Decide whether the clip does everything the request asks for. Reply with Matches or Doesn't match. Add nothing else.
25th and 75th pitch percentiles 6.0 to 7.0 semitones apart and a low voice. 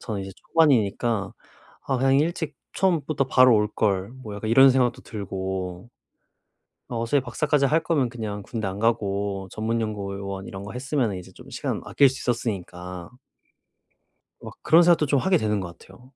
Doesn't match